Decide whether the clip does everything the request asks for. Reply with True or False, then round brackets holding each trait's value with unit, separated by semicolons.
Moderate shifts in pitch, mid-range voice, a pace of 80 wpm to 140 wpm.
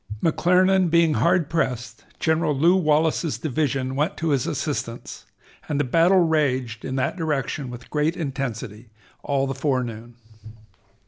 True (4.2 semitones; 150 Hz; 135 wpm)